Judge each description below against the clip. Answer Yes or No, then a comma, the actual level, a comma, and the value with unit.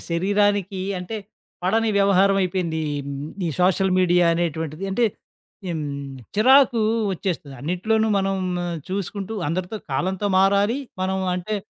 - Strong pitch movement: No, narrow, 2.5 semitones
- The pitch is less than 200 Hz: Yes, high, 190 Hz